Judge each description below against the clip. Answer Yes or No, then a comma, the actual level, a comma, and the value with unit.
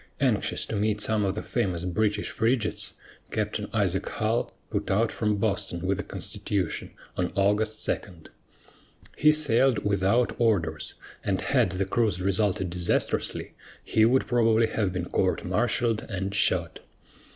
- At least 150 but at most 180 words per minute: No, average, 140 wpm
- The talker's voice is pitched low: Yes, low, 105 Hz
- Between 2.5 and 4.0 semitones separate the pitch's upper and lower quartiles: Yes, average, 3.1 semitones